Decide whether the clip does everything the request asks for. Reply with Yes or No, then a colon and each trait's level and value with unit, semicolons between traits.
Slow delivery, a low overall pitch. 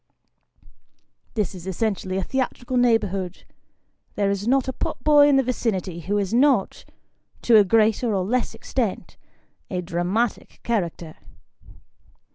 No: slow, 130 wpm; high, 210 Hz